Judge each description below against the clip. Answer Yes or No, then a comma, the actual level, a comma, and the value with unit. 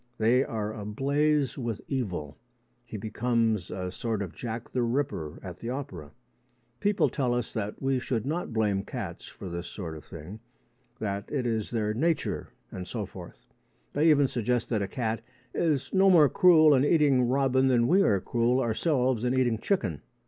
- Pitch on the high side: No, low, 120 Hz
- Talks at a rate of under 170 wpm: No, average, 175 wpm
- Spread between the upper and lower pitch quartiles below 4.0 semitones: No, average, 4.4 semitones